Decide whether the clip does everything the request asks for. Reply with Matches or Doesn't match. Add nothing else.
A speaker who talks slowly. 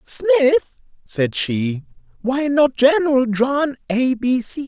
Matches